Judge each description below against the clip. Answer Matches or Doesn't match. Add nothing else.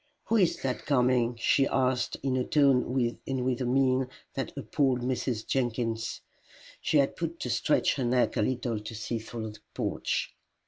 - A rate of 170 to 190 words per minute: Matches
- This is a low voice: Matches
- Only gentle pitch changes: Matches